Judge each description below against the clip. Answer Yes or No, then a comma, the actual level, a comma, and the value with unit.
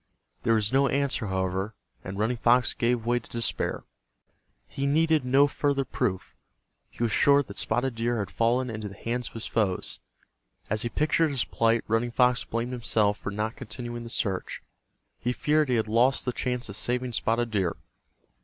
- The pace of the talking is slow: No, average, 180 wpm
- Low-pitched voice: Yes, low, 120 Hz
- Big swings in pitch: No, narrow, 2.6 semitones